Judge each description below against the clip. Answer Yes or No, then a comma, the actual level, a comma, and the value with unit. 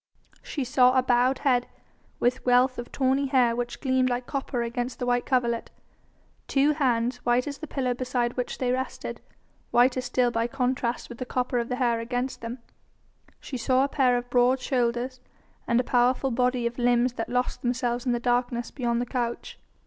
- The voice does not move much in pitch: Yes, narrow, 1.1 semitones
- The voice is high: Yes, very high, 250 Hz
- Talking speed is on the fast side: No, average, 185 wpm